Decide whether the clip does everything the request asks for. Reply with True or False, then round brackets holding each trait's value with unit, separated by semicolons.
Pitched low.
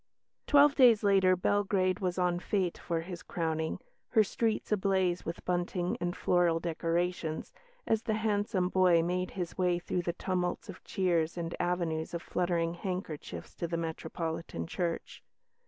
False (180 Hz)